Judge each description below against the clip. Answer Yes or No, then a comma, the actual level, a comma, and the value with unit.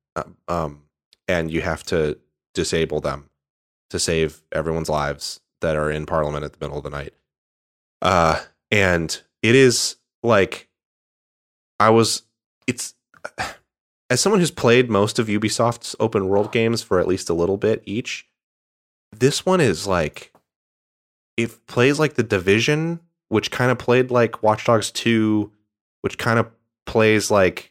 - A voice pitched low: Yes, low, 105 Hz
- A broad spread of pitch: Yes, wide, 7.5 semitones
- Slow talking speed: No, average, 145 wpm